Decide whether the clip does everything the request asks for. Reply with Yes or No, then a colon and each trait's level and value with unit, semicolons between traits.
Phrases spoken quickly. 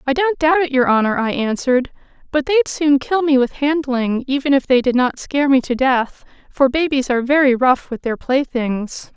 Yes: fast, 225 wpm